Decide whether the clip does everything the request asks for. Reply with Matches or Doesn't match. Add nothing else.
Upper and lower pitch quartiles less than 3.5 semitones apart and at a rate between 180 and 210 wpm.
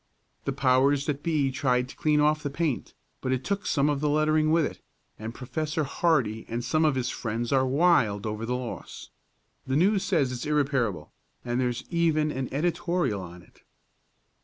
Doesn't match